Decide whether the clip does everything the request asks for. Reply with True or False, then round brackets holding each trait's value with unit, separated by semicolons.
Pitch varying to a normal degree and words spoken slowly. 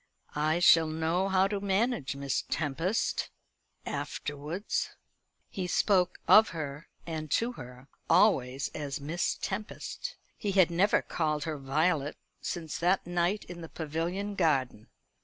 True (4.4 semitones; 130 wpm)